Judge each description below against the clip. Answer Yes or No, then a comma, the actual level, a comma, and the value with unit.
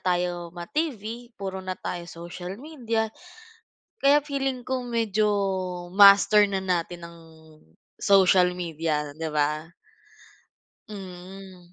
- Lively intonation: No, average, 4.2 semitones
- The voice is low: No, high, 190 Hz